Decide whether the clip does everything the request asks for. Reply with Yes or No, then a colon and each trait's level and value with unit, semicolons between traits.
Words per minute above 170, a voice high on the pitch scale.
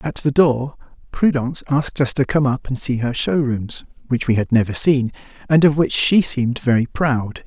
No: average, 200 wpm; low, 135 Hz